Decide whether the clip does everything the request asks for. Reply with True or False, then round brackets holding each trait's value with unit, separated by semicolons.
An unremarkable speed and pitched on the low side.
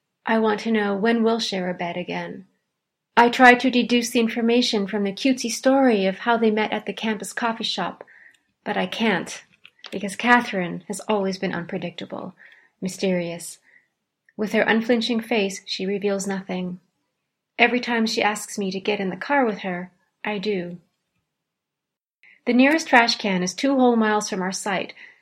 False (170 wpm; 210 Hz)